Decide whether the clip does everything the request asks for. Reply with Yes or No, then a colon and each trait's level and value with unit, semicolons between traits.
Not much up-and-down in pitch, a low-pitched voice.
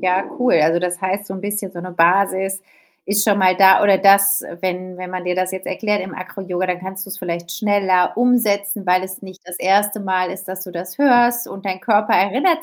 No: narrow, 1.8 semitones; high, 190 Hz